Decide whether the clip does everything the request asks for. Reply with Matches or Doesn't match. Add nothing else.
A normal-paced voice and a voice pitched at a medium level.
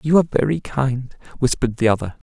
Doesn't match